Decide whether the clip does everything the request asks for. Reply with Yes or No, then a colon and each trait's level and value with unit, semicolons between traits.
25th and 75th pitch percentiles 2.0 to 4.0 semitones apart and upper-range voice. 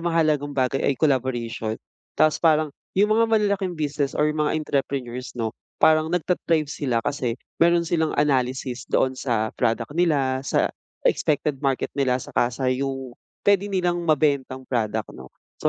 No: average, 3.7 semitones; medium, 140 Hz